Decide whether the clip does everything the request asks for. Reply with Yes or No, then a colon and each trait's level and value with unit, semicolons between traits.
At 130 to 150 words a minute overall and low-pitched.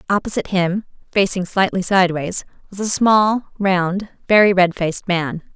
No: average, 140 wpm; high, 190 Hz